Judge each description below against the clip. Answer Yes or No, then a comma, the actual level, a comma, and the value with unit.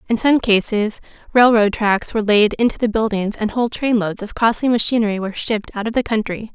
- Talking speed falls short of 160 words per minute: No, average, 200 wpm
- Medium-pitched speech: No, high, 220 Hz